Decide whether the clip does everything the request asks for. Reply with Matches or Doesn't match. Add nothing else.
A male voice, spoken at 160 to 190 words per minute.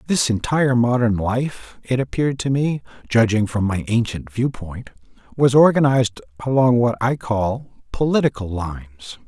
Doesn't match